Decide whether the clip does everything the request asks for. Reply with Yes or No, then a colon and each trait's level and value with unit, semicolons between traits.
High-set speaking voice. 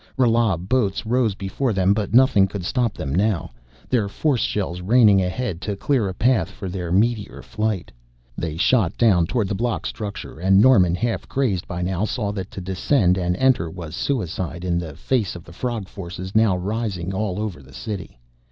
No: low, 100 Hz